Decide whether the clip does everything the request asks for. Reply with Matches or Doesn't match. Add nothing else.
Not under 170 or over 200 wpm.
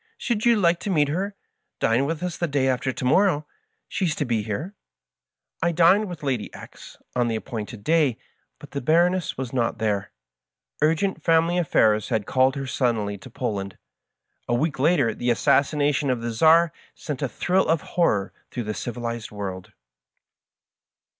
Matches